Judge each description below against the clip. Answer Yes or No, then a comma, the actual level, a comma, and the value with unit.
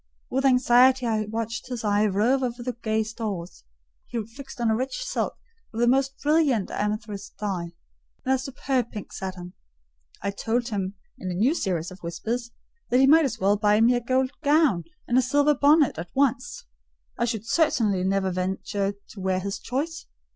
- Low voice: No, high, 230 Hz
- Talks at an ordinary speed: Yes, average, 185 wpm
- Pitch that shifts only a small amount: No, average, 4.7 semitones